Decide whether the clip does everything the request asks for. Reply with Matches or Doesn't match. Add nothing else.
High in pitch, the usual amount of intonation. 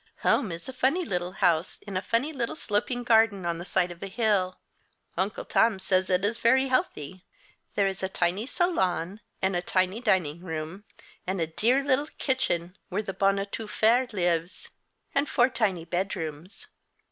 Matches